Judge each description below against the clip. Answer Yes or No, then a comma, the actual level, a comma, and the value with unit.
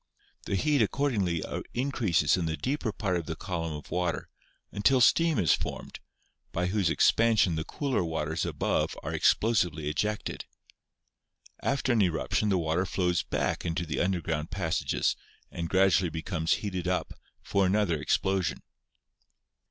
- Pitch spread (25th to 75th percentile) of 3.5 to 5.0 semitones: Yes, average, 4.4 semitones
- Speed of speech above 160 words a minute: No, average, 145 wpm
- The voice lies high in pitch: No, very low, 90 Hz